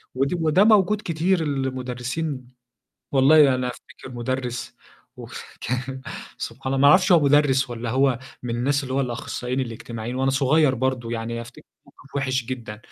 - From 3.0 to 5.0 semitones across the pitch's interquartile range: No, narrow, 2.6 semitones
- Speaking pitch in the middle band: No, low, 130 Hz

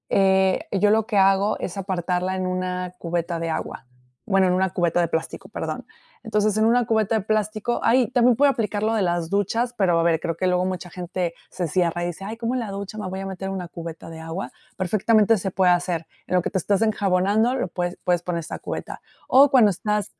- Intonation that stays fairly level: No, average, 3.3 semitones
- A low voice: No, high, 190 Hz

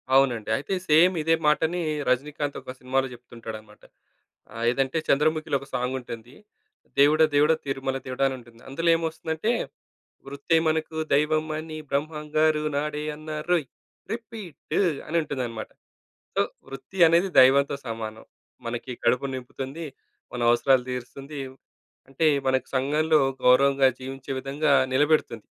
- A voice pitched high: No, medium, 140 Hz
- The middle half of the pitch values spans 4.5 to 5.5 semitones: No, average, 3.4 semitones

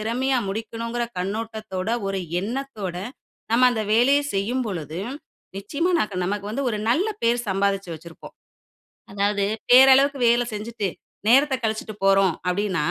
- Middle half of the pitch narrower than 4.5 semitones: Yes, average, 3.8 semitones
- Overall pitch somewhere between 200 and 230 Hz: Yes, high, 215 Hz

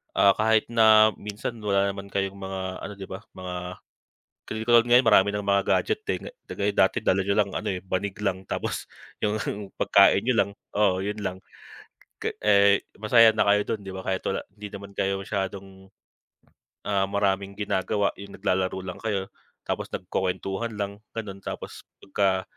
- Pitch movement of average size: No, narrow, 1.6 semitones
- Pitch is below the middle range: Yes, low, 100 Hz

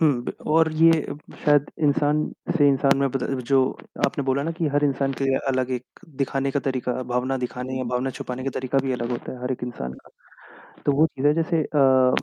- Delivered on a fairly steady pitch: Yes, narrow, 2.2 semitones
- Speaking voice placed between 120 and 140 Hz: Yes, low, 135 Hz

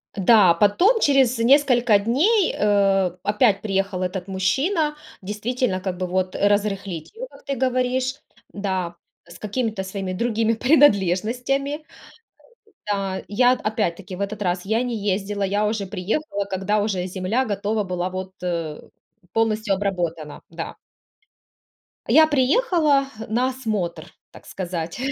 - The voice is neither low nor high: No, high, 205 Hz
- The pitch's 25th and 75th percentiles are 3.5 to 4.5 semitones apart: No, average, 5.0 semitones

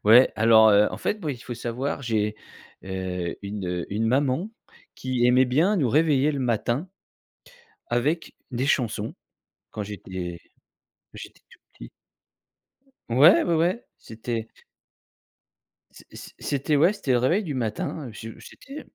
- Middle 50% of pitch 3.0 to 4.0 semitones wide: No, average, 5.1 semitones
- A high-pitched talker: No, low, 125 Hz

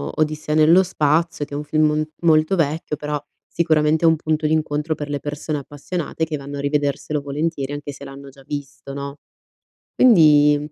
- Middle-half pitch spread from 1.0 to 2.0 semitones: Yes, narrow, 1.6 semitones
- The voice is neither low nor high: Yes, medium, 150 Hz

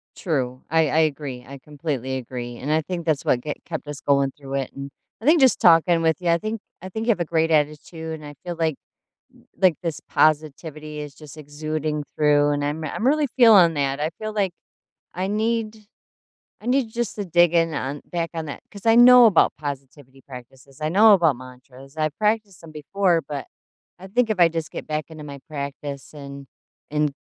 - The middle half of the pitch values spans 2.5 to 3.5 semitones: No, average, 4.2 semitones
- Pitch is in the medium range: Yes, medium, 155 Hz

